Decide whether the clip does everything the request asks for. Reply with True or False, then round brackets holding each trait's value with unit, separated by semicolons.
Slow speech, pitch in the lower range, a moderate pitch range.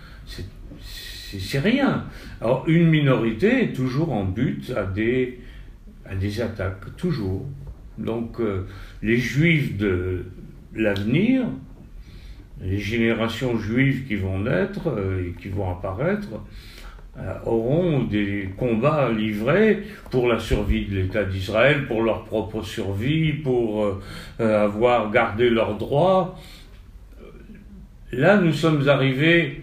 False (120 wpm; 115 Hz; 5.9 semitones)